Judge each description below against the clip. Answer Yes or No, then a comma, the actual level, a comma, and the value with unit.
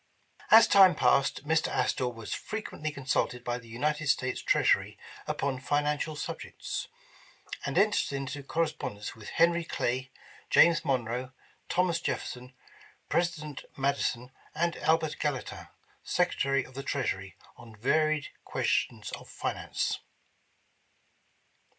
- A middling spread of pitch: Yes, average, 4.0 semitones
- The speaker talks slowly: Yes, slow, 115 wpm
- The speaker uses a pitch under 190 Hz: Yes, medium, 140 Hz